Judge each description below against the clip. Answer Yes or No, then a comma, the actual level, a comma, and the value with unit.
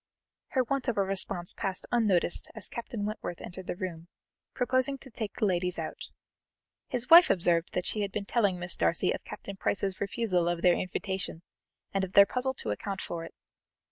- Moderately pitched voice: No, high, 195 Hz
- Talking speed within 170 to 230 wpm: Yes, average, 185 wpm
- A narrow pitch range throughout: No, average, 4.3 semitones